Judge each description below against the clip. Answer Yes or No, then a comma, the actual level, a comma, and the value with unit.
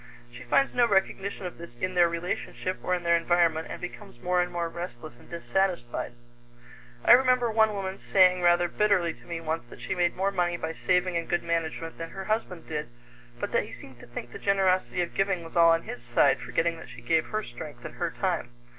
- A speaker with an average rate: No, fast, 220 wpm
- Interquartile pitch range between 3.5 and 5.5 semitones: No, narrow, 2.4 semitones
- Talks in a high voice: No, medium, 175 Hz